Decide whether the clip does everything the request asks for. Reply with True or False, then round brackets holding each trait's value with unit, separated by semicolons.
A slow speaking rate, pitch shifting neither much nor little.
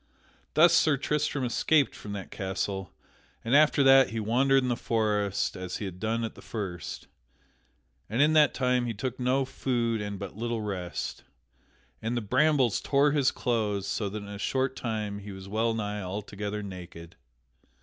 False (170 wpm; 4.4 semitones)